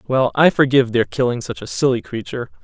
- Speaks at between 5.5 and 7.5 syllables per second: Yes, 6.4 syllables/s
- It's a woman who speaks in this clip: No, male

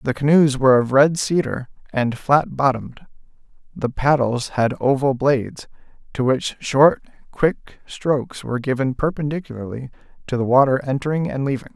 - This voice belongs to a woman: No, male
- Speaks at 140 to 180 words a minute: Yes, average, 145 wpm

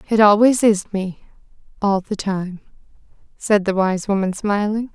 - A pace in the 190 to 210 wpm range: No, average, 145 wpm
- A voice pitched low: No, high, 200 Hz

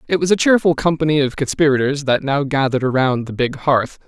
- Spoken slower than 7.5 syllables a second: Yes, 6.0 syllables/s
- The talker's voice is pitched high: No, medium, 140 Hz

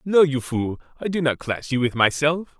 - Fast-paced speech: Yes, fast, 230 wpm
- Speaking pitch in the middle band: Yes, medium, 145 Hz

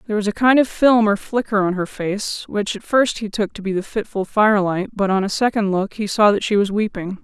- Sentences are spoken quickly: Yes, fast, 265 wpm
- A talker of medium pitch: No, high, 205 Hz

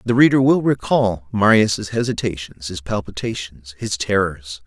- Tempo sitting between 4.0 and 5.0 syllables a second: Yes, 4.5 syllables/s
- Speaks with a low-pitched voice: Yes, low, 105 Hz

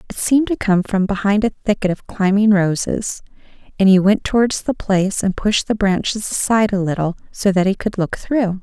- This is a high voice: Yes, high, 200 Hz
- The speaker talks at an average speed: No, fast, 210 wpm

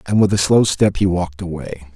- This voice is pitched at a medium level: No, very low, 90 Hz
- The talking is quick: Yes, fast, 245 wpm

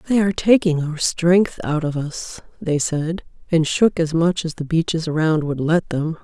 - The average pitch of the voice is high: No, medium, 165 Hz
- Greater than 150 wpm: Yes, average, 200 wpm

